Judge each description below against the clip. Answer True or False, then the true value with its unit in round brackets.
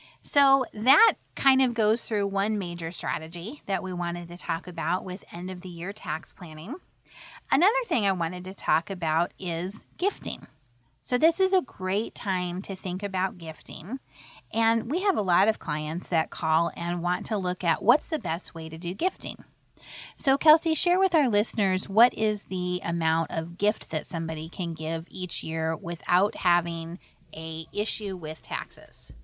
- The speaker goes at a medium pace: True (175 wpm)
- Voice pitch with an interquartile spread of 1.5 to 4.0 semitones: False (4.7 semitones)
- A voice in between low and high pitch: True (180 Hz)